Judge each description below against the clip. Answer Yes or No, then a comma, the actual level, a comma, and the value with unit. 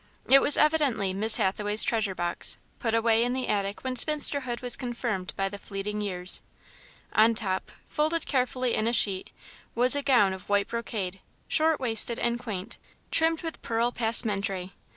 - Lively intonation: No, average, 4.2 semitones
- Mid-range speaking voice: No, high, 230 Hz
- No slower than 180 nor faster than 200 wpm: No, average, 165 wpm